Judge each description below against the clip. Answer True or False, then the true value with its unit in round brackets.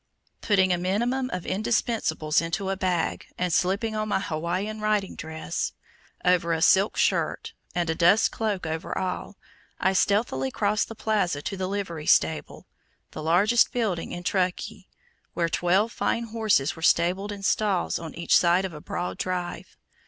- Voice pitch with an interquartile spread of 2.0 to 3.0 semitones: False (3.5 semitones)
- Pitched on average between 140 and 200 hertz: True (185 Hz)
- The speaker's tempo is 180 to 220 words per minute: False (160 wpm)